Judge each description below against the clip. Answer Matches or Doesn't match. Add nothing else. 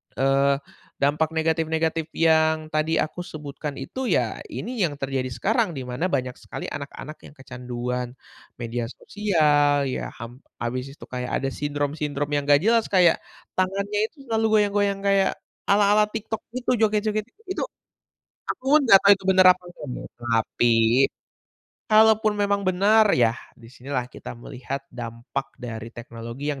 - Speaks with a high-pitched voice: Doesn't match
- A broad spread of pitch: Matches